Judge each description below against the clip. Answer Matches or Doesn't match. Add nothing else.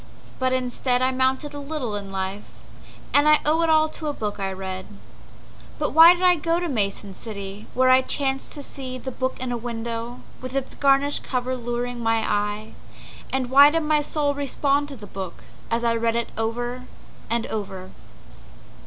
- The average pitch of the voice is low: Doesn't match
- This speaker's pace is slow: Doesn't match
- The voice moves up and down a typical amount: Matches